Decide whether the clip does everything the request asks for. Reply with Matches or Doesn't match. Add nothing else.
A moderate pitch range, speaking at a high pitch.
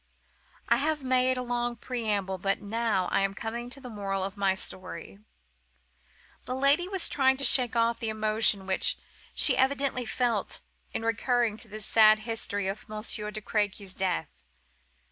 Matches